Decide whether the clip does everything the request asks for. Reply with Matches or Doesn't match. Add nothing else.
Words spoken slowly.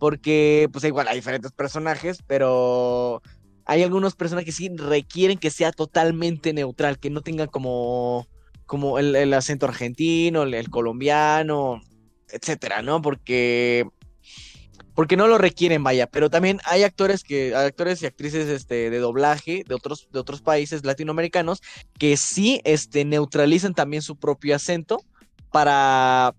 Doesn't match